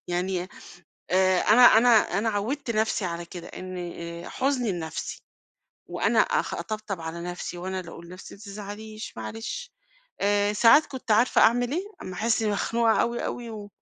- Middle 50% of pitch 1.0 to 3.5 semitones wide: No, average, 4.2 semitones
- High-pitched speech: Yes, high, 205 Hz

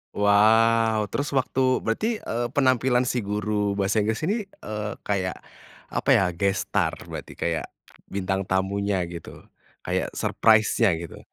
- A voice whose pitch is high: No, low, 105 Hz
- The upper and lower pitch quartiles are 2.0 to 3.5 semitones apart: Yes, average, 2.9 semitones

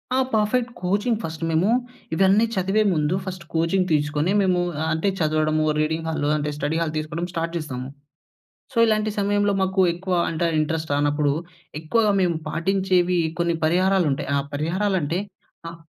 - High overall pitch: No, medium, 170 Hz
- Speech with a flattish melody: No, average, 3.6 semitones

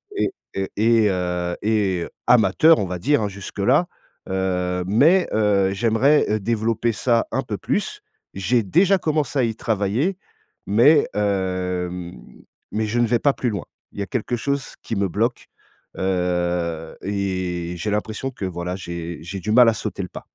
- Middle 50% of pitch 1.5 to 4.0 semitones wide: No, average, 4.5 semitones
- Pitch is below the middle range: Yes, low, 100 Hz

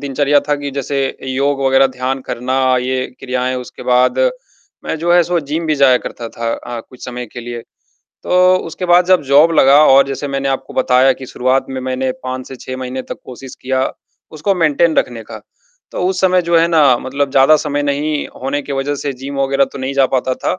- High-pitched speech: No, low, 135 Hz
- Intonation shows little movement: Yes, narrow, 2.3 semitones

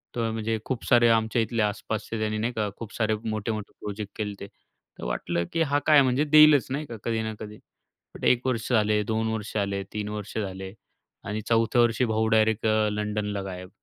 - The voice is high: No, low, 110 Hz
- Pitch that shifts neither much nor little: No, narrow, 1.8 semitones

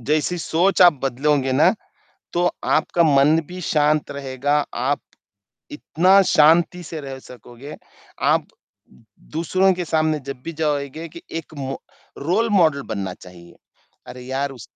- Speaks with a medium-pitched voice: Yes, medium, 150 Hz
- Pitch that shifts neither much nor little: Yes, average, 3.7 semitones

